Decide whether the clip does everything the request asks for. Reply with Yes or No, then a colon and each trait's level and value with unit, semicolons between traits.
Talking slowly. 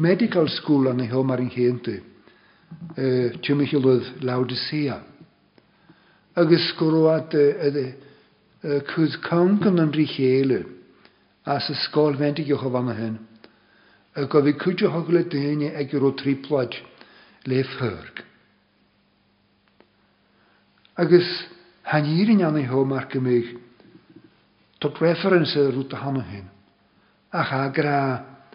Yes: slow, 115 wpm